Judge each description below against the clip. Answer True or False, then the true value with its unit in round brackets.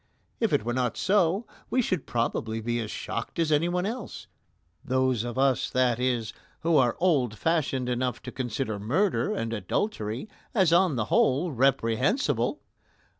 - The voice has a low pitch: True (130 Hz)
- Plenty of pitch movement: True (6.3 semitones)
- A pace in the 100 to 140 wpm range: False (155 wpm)